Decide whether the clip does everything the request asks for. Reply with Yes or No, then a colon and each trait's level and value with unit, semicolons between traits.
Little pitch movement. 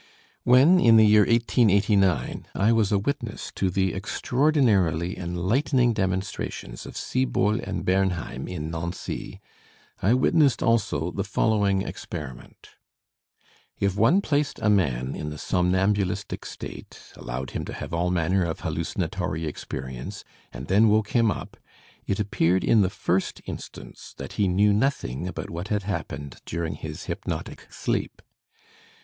No: average, 4.3 semitones